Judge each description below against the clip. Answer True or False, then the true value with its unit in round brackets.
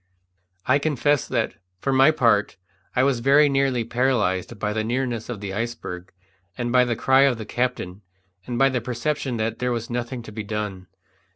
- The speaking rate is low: False (185 wpm)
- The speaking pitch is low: True (120 Hz)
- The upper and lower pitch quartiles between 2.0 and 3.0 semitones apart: False (3.4 semitones)